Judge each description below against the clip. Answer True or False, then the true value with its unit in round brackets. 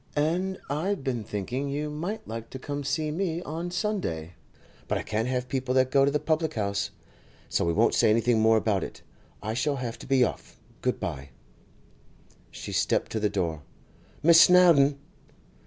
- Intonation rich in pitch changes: True (6.1 semitones)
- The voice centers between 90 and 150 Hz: True (135 Hz)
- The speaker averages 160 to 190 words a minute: True (185 wpm)